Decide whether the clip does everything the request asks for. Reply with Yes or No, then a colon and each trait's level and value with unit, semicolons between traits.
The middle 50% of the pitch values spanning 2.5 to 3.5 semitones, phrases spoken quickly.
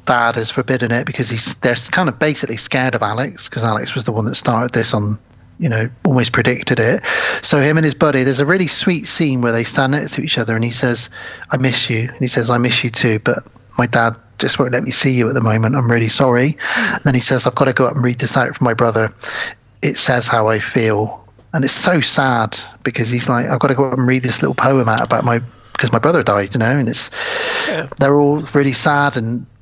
Yes: average, 2.8 semitones; fast, 255 wpm